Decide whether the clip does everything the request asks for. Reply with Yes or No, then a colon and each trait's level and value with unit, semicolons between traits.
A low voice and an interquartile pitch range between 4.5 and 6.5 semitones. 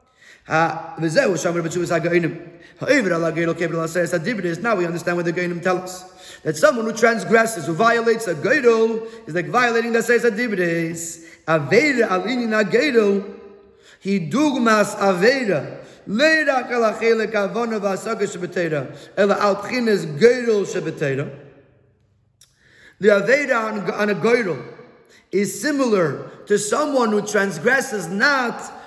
No: high, 200 Hz; average, 5.0 semitones